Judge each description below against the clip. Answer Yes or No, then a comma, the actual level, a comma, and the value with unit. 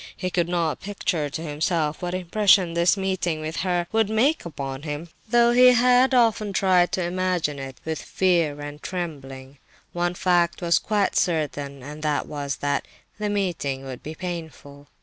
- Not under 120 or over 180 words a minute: Yes, average, 170 wpm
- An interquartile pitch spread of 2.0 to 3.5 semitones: No, average, 4.3 semitones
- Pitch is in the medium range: Yes, medium, 170 Hz